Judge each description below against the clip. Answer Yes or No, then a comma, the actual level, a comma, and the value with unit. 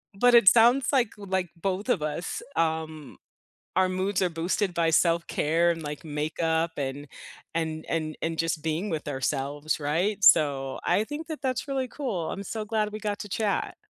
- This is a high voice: No, medium, 170 Hz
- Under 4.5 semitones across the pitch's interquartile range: No, average, 5.0 semitones